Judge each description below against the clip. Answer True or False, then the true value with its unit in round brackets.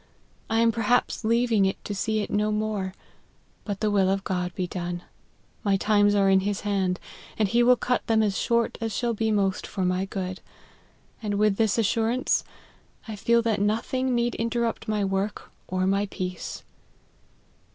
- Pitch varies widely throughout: False (2.8 semitones)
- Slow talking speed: False (180 wpm)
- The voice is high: True (210 Hz)